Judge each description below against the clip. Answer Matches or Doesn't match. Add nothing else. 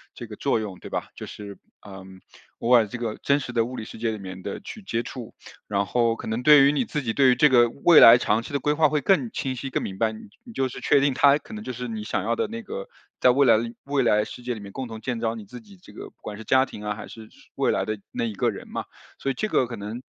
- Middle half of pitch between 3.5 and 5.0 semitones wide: Matches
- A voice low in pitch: Matches